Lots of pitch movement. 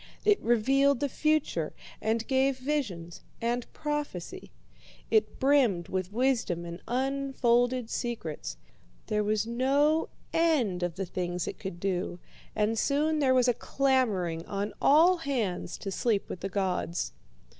Yes: wide, 6.4 semitones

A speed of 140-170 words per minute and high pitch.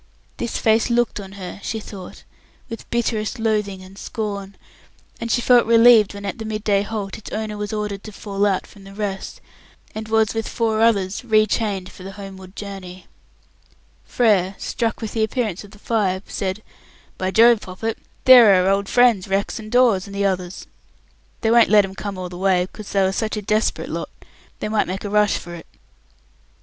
No: average, 195 wpm; high, 205 Hz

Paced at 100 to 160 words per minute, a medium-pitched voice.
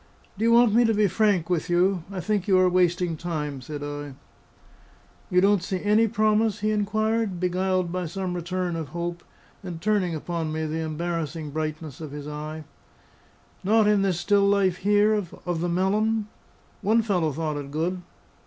No: average, 175 wpm; medium, 180 Hz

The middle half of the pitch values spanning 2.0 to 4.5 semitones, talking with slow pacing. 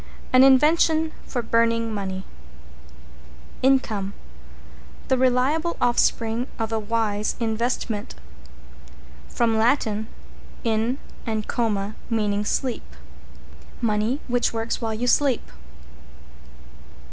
Yes: average, 2.8 semitones; slow, 90 wpm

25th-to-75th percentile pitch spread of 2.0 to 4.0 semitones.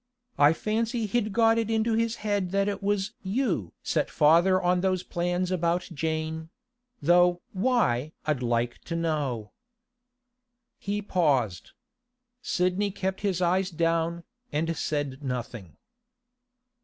No: average, 4.7 semitones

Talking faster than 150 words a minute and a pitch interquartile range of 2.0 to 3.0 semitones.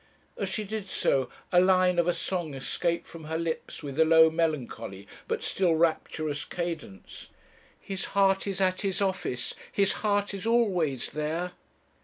No: average, 160 wpm; average, 3.6 semitones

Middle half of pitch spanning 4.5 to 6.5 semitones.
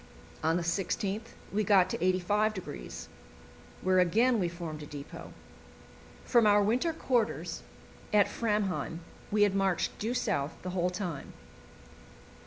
No: average, 3.5 semitones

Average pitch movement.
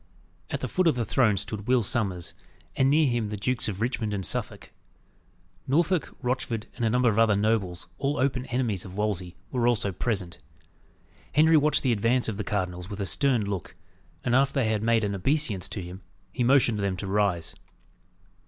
Yes: average, 4.3 semitones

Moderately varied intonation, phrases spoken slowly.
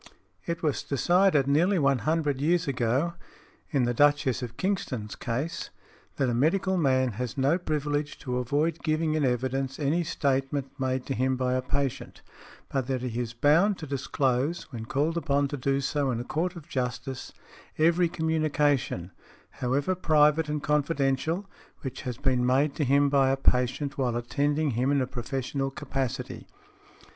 No: average, 3.2 semitones; average, 165 wpm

